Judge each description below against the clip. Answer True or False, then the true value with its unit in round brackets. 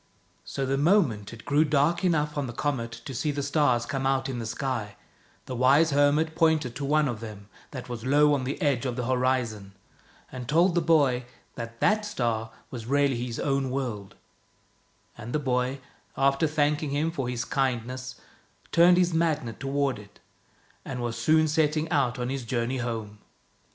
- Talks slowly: False (180 wpm)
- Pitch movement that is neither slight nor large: True (3.6 semitones)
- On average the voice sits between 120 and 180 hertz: True (135 Hz)